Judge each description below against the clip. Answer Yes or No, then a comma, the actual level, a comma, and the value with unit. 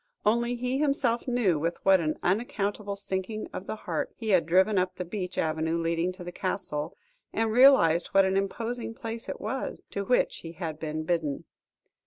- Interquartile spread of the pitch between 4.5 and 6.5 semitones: Yes, average, 5.1 semitones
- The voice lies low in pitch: No, high, 190 Hz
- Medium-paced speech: Yes, average, 185 wpm